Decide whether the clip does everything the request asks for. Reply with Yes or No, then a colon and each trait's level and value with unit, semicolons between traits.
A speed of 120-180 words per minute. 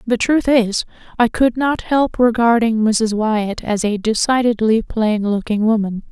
Yes: average, 155 wpm